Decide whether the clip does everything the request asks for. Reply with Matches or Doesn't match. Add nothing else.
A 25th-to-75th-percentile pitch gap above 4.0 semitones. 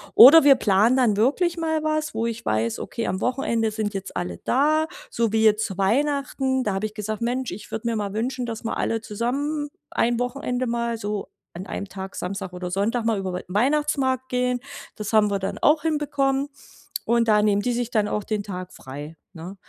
Matches